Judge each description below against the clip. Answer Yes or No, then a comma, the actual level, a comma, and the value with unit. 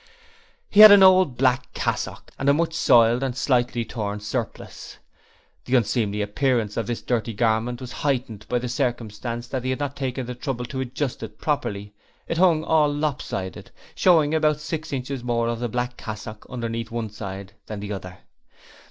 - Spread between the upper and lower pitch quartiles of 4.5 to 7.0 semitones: No, average, 3.8 semitones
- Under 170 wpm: No, average, 185 wpm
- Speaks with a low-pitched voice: Yes, low, 125 Hz